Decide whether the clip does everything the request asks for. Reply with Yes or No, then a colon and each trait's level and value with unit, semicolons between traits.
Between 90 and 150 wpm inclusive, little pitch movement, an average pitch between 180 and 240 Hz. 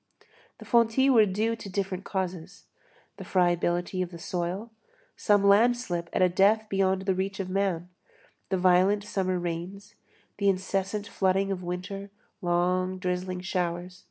Yes: average, 145 wpm; narrow, 1.8 semitones; high, 190 Hz